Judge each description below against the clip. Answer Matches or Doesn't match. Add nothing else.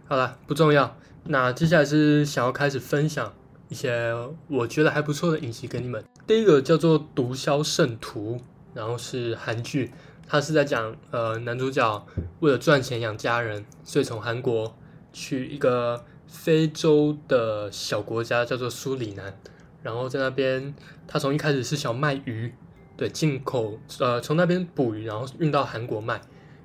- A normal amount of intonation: Matches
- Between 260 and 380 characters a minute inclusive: Doesn't match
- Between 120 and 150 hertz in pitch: Matches